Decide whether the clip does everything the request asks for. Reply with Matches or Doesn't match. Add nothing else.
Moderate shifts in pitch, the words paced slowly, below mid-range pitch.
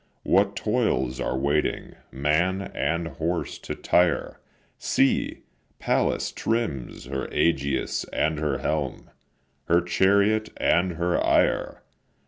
Matches